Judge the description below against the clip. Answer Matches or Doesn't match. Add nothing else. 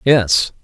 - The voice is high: Doesn't match